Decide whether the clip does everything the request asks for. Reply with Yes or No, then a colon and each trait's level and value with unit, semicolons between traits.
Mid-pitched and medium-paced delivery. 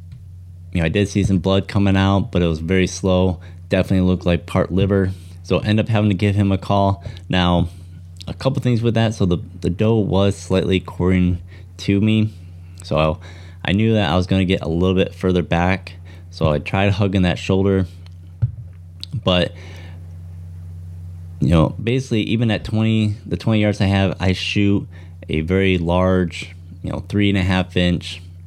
No: very low, 90 Hz; average, 185 wpm